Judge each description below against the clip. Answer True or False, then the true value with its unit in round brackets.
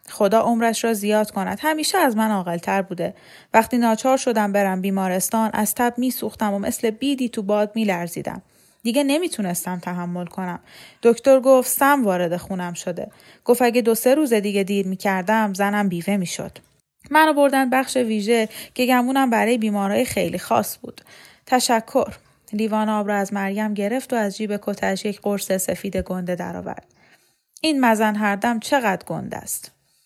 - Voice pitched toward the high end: True (215 Hz)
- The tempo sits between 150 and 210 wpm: True (155 wpm)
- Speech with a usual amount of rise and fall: True (3.7 semitones)